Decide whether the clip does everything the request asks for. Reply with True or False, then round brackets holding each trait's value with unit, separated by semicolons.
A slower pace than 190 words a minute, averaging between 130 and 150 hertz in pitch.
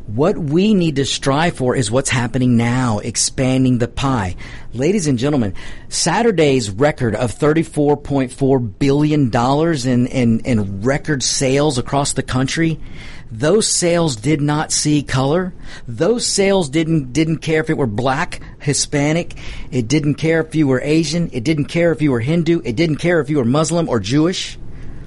True (165 wpm; 140 Hz)